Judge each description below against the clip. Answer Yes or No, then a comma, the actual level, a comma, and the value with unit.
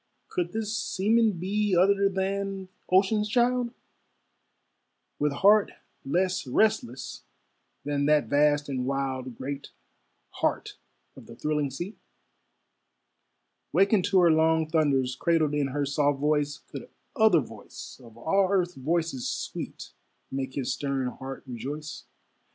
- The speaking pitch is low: No, medium, 155 Hz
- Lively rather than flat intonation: Yes, wide, 6.0 semitones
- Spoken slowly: Yes, slow, 120 wpm